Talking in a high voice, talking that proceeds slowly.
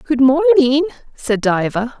Yes: very high, 275 Hz; slow, 120 wpm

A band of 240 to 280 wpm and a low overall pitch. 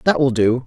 Yes: fast, 270 wpm; low, 130 Hz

